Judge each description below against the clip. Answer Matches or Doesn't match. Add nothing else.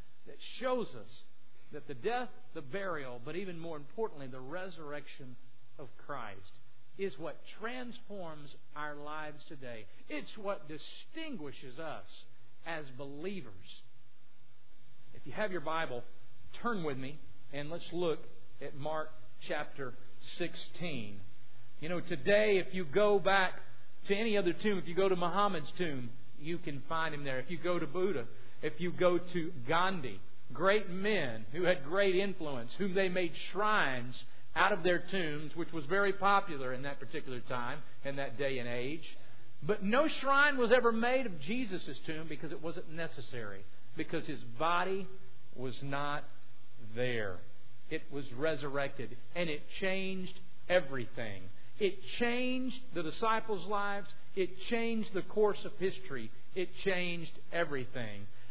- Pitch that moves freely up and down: Matches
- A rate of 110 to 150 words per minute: Matches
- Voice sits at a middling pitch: Matches